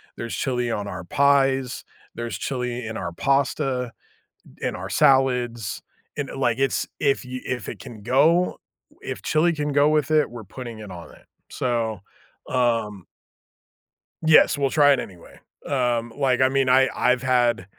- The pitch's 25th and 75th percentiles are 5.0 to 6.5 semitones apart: No, average, 2.8 semitones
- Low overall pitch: Yes, low, 125 Hz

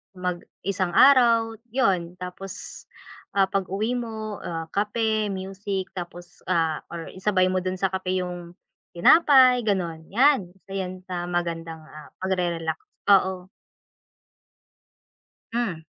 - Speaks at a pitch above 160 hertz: Yes, medium, 185 Hz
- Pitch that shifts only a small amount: No, average, 3.1 semitones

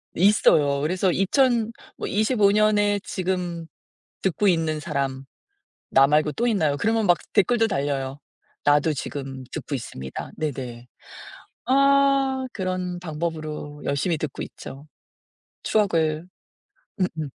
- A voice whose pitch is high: No, medium, 170 Hz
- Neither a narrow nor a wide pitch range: No, wide, 6.0 semitones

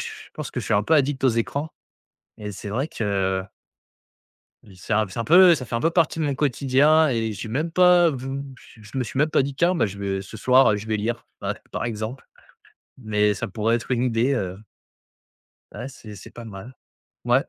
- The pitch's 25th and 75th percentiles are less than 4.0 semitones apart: No, average, 4.9 semitones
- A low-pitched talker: Yes, low, 120 Hz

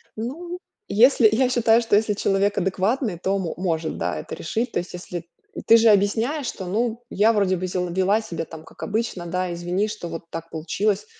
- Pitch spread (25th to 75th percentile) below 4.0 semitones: No, average, 4.3 semitones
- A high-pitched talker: Yes, high, 200 Hz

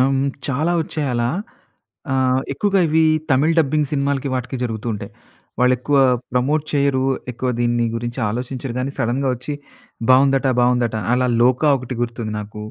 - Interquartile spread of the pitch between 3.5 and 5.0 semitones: No, narrow, 2.5 semitones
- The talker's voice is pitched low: Yes, low, 130 Hz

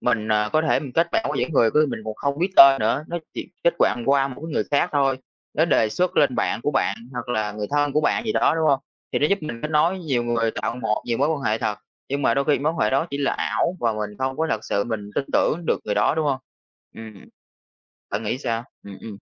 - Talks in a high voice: No, low, 135 Hz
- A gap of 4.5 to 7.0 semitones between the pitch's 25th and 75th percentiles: Yes, wide, 5.4 semitones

